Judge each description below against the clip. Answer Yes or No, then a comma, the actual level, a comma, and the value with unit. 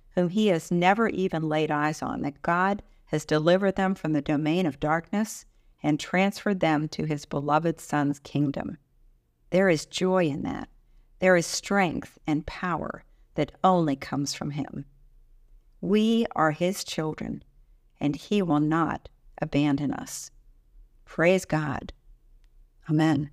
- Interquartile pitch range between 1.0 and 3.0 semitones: No, average, 4.2 semitones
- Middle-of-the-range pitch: Yes, medium, 155 Hz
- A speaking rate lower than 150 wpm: Yes, average, 140 wpm